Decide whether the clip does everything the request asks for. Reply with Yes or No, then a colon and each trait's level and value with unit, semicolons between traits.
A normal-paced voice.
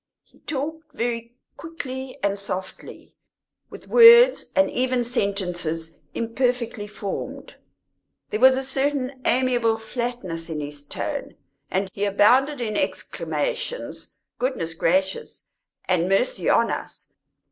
No: slow, 115 wpm